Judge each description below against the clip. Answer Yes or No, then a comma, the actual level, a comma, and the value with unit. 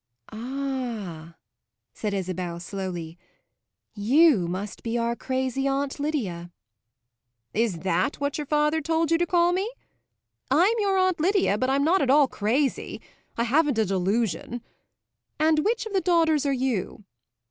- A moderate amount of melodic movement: No, wide, 7.5 semitones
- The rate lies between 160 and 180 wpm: No, average, 145 wpm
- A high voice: Yes, very high, 265 Hz